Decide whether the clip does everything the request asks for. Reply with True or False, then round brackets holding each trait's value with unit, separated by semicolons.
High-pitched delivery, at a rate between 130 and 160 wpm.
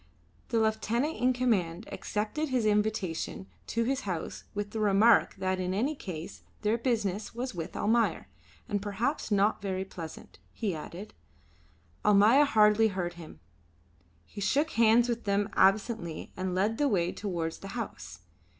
True (210 Hz; 150 wpm)